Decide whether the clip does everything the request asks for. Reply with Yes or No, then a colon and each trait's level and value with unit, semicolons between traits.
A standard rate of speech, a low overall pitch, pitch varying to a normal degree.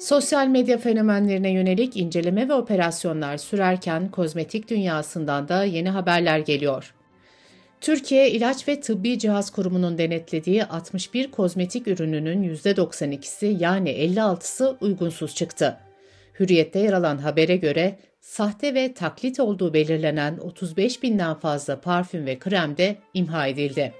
No: average, 120 wpm; medium, 180 Hz; average, 4.6 semitones